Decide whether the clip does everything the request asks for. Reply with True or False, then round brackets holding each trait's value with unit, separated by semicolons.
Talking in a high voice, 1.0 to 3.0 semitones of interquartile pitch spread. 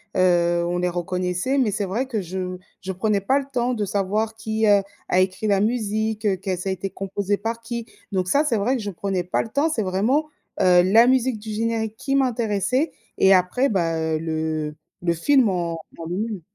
False (200 Hz; 4.0 semitones)